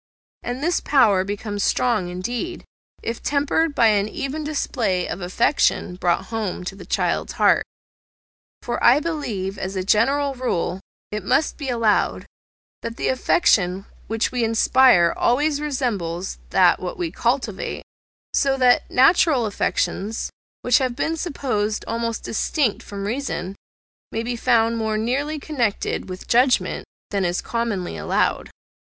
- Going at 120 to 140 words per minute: Yes, slow, 135 wpm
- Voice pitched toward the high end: Yes, high, 230 Hz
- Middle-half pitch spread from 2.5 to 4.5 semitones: No, average, 5.1 semitones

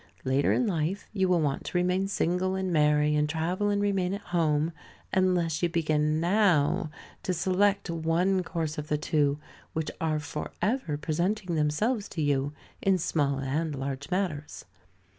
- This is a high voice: No, medium, 165 Hz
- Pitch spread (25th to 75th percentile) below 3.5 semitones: No, average, 3.8 semitones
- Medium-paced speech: Yes, average, 160 wpm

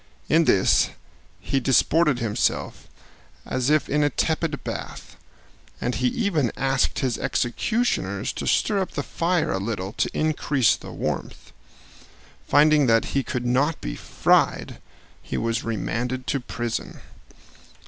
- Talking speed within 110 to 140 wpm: Yes, slow, 135 wpm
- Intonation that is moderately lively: Yes, average, 4.4 semitones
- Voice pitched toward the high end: No, low, 135 Hz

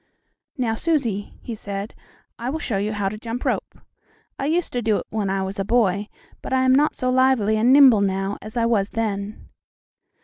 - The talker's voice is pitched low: No, high, 220 Hz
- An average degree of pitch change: Yes, average, 4.0 semitones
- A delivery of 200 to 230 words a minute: Yes, fast, 205 wpm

